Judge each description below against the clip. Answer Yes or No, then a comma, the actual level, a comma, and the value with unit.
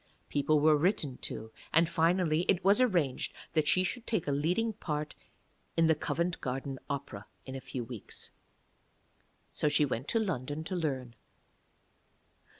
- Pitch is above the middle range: No, medium, 155 Hz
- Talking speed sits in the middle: Yes, average, 150 wpm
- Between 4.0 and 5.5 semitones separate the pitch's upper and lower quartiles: Yes, average, 4.7 semitones